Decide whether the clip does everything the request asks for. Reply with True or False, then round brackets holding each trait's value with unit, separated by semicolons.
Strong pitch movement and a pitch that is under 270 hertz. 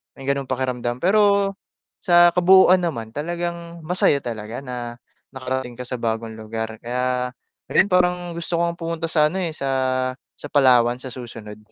True (6.1 semitones; 135 Hz)